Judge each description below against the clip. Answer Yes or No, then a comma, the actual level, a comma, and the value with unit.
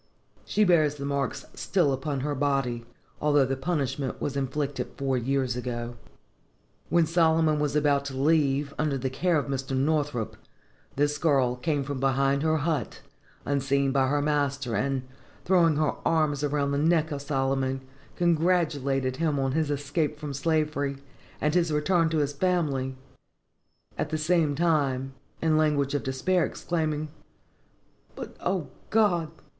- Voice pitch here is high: No, medium, 145 Hz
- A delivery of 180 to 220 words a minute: No, average, 150 wpm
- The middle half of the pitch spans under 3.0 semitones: Yes, narrow, 2.6 semitones